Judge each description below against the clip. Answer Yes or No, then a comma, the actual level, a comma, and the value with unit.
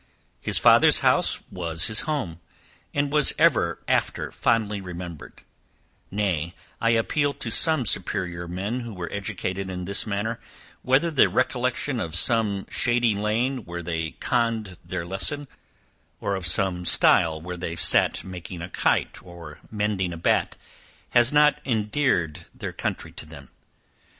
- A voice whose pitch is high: No, low, 100 Hz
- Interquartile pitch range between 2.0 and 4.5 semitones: No, average, 5.3 semitones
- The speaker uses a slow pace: No, average, 145 wpm